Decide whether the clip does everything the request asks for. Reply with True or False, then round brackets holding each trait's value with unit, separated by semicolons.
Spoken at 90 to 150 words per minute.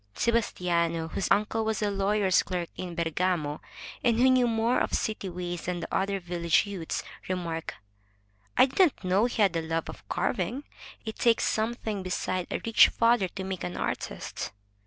False (175 wpm)